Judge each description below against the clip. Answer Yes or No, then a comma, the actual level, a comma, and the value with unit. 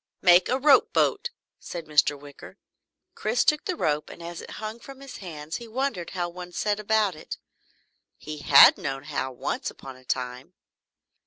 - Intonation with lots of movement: Yes, wide, 6.9 semitones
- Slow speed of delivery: No, average, 175 wpm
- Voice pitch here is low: No, medium, 175 Hz